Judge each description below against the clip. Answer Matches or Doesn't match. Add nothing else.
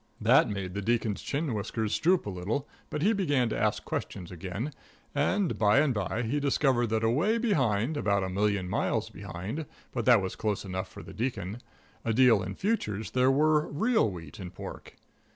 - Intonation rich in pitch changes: Matches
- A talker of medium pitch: Doesn't match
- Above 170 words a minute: Matches